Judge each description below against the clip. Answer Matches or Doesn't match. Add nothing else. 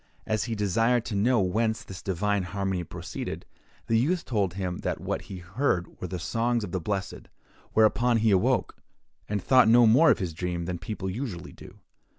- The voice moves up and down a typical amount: Matches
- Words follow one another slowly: Doesn't match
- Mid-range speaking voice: Doesn't match